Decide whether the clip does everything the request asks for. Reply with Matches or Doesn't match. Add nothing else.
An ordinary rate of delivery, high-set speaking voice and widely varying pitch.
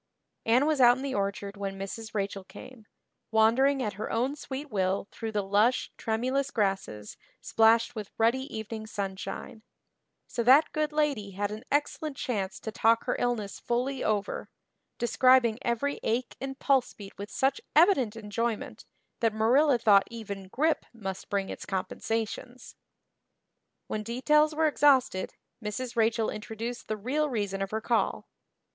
Doesn't match